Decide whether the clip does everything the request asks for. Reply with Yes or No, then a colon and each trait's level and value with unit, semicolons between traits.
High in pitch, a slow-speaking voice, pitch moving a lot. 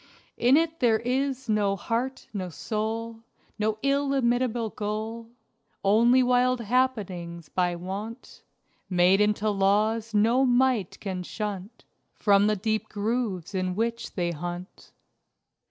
No: high, 215 Hz; slow, 120 wpm; average, 3.7 semitones